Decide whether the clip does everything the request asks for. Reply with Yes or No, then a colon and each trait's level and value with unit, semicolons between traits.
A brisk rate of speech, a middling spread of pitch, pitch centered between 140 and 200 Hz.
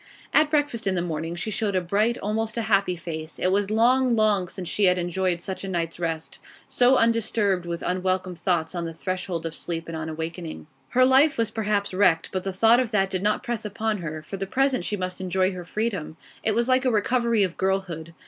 Yes: fast, 225 wpm; average, 4.3 semitones; high, 190 Hz